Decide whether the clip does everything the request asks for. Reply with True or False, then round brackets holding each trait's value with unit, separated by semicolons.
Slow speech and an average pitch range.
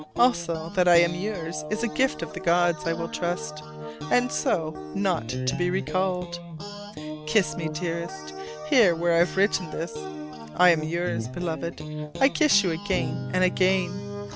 False (165 wpm; 3.1 semitones)